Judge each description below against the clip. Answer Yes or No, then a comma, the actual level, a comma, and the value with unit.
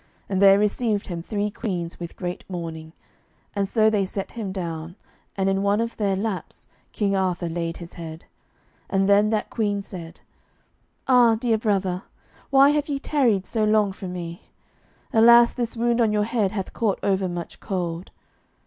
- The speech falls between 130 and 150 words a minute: No, average, 170 wpm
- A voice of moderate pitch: No, high, 200 Hz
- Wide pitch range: No, average, 3.6 semitones